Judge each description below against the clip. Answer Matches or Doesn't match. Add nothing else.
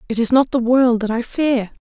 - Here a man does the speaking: Doesn't match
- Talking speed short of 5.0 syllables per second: Doesn't match